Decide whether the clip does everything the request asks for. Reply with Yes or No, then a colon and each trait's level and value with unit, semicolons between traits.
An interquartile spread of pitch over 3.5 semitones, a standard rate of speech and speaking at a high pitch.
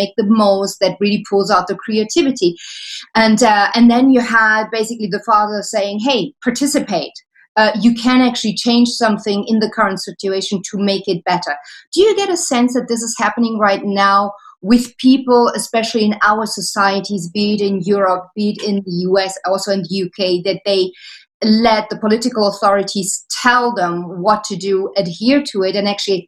No: average, 2.9 semitones; average, 185 wpm; high, 210 Hz